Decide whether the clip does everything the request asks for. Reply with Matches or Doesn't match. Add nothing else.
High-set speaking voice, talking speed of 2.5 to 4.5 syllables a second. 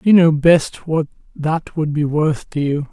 Doesn't match